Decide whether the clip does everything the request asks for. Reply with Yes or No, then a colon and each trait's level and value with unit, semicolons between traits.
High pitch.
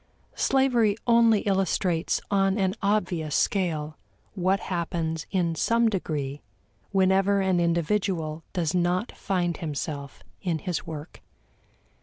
No: medium, 180 Hz